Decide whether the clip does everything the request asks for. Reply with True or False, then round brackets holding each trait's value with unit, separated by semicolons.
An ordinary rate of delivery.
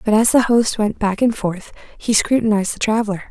False (220 wpm)